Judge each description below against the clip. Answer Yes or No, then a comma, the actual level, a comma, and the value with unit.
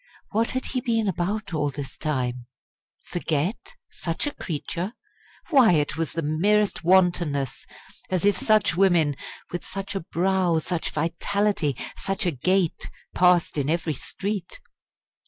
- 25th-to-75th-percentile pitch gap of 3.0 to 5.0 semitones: Yes, average, 4.2 semitones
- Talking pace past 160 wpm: No, slow, 135 wpm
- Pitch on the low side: No, medium, 175 Hz